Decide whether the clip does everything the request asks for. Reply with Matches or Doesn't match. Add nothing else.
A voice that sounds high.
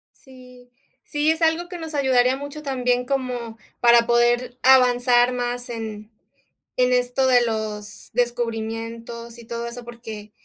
Matches